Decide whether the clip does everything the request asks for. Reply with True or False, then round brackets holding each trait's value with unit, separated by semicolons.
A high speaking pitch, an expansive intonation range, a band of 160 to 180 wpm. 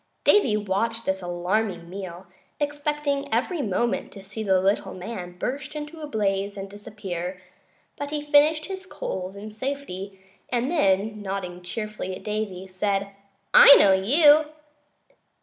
False (210 Hz; 6.8 semitones; 140 wpm)